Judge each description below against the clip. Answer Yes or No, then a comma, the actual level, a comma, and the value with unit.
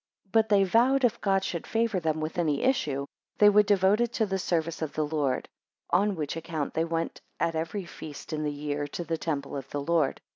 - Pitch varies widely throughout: No, average, 4.8 semitones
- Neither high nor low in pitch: Yes, medium, 165 Hz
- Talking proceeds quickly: Yes, fast, 225 wpm